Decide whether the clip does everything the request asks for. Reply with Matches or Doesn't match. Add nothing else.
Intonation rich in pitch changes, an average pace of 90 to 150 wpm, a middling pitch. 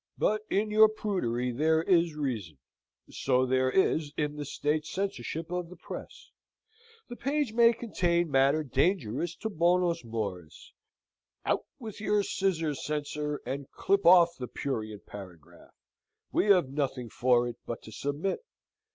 Matches